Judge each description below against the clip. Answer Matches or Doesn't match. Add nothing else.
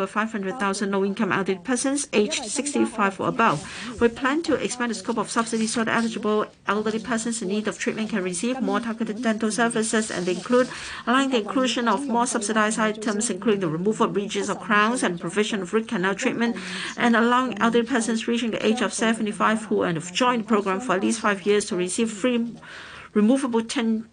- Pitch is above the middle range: Matches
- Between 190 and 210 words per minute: Matches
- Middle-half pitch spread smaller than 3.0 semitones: Matches